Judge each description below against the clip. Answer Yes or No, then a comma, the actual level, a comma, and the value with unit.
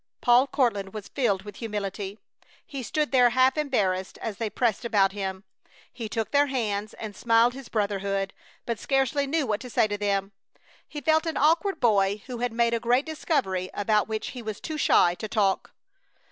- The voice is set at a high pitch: Yes, high, 225 Hz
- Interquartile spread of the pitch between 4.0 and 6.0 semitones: Yes, average, 4.4 semitones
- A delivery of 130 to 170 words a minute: No, average, 190 wpm